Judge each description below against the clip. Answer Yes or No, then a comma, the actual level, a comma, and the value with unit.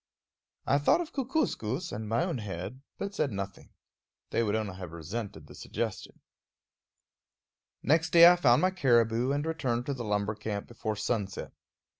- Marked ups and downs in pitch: Yes, wide, 6.4 semitones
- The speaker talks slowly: No, average, 160 wpm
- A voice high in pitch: No, low, 120 Hz